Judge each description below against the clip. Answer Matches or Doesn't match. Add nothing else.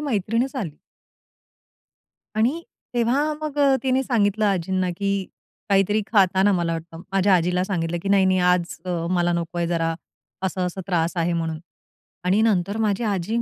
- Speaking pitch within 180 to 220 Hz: Matches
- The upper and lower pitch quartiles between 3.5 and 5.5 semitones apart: Matches